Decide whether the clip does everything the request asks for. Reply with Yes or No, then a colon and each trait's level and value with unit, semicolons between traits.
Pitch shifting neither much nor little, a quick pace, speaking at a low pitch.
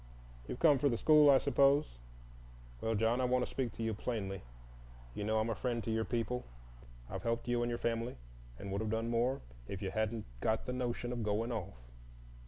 No: narrow, 2.2 semitones; fast, 210 wpm; low, 115 Hz